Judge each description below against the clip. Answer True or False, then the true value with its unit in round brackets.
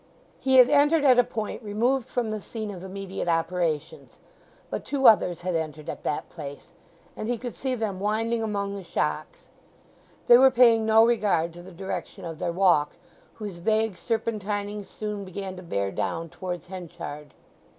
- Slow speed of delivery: False (170 wpm)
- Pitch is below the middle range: False (200 Hz)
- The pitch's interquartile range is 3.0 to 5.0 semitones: True (4.5 semitones)